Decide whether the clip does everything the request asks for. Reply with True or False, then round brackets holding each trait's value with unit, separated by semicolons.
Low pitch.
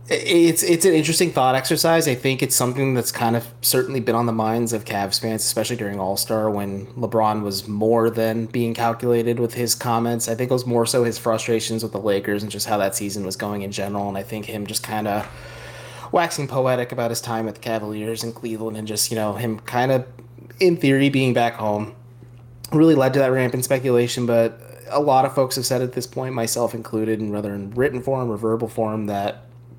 True (115 Hz)